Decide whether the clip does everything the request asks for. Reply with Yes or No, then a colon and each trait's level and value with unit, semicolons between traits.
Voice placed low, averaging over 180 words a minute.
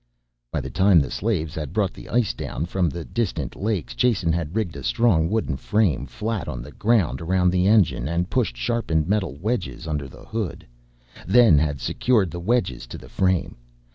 Yes: very low, 90 Hz; average, 190 wpm